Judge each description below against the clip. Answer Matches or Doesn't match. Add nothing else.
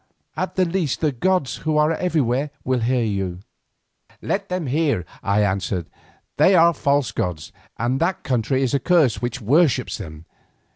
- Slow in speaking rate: Doesn't match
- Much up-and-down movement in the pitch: Matches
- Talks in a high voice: Doesn't match